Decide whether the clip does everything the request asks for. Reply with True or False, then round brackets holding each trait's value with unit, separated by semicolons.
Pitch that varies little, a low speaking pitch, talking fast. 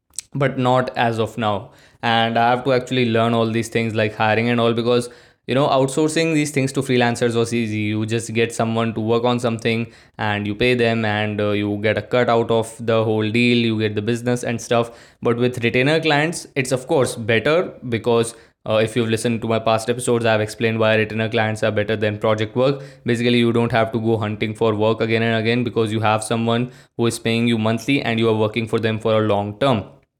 True (1.7 semitones; 115 Hz; 230 wpm)